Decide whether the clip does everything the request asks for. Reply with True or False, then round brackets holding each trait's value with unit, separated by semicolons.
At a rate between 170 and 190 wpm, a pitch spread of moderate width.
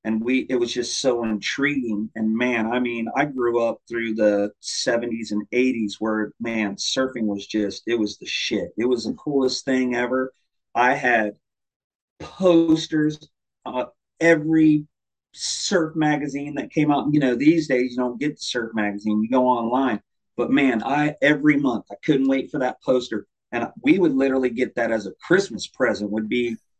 True (180 wpm; 4.3 semitones)